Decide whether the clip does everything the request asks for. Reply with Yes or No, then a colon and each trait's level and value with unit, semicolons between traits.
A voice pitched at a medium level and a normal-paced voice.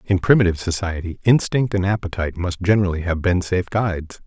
No: very low, 95 Hz; average, 170 wpm